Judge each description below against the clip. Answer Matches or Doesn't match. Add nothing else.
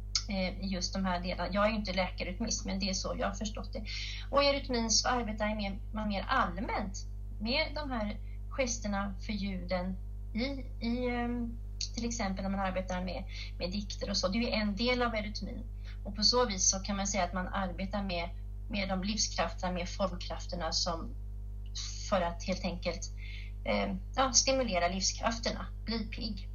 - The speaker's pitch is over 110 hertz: Matches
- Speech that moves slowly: Doesn't match